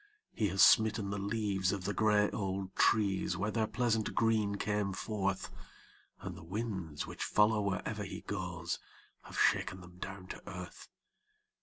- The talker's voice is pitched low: Yes, low, 100 Hz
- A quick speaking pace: No, average, 155 wpm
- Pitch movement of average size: No, narrow, 2.1 semitones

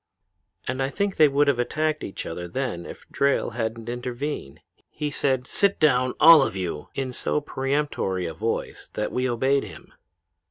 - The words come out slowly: No, average, 170 wpm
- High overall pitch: No, low, 130 Hz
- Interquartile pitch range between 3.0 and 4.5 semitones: Yes, average, 4.2 semitones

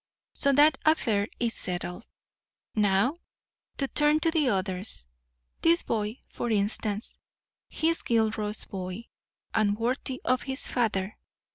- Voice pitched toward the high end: Yes, high, 225 Hz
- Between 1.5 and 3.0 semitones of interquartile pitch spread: No, average, 5.0 semitones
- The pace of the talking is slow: Yes, slow, 125 wpm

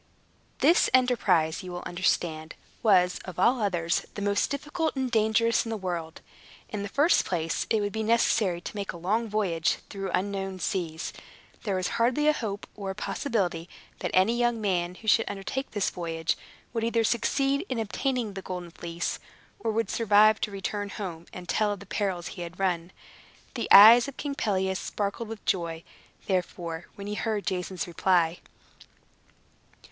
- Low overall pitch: No, high, 200 Hz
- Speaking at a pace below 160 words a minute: No, average, 170 wpm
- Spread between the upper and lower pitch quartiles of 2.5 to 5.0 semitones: Yes, average, 4.0 semitones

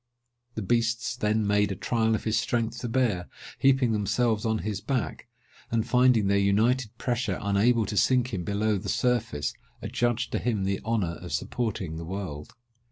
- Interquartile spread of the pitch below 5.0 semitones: Yes, average, 3.3 semitones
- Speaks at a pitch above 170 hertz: No, low, 110 Hz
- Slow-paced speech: No, average, 170 wpm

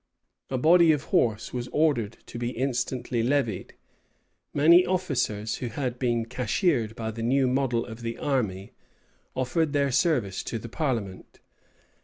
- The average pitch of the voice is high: No, low, 125 Hz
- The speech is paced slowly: No, average, 145 wpm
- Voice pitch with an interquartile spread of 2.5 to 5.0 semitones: Yes, average, 3.7 semitones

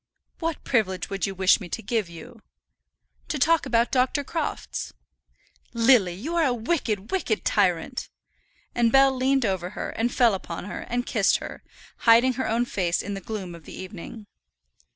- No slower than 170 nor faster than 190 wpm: Yes, average, 175 wpm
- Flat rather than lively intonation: No, average, 5.1 semitones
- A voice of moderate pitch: No, high, 230 Hz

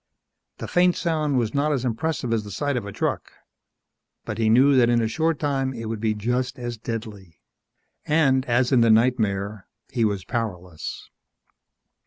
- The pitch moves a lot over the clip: No, average, 3.7 semitones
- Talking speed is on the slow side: No, average, 175 wpm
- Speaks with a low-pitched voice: Yes, low, 120 Hz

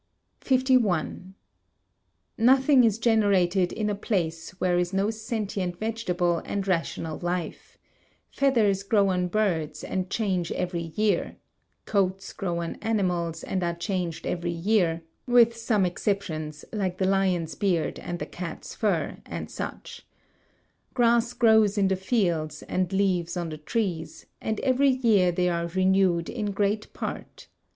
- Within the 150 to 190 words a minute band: No, average, 140 wpm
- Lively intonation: No, average, 3.8 semitones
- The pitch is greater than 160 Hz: Yes, high, 190 Hz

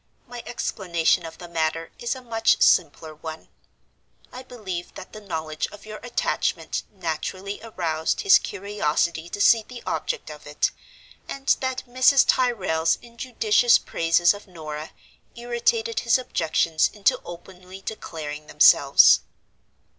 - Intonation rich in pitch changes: Yes, wide, 6.5 semitones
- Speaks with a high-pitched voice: Yes, high, 195 Hz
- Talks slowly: Yes, slow, 130 wpm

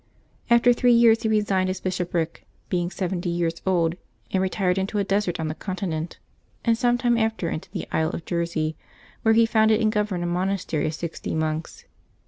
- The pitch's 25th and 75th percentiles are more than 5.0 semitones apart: No, average, 4.3 semitones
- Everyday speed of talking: Yes, average, 185 wpm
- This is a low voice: No, medium, 185 Hz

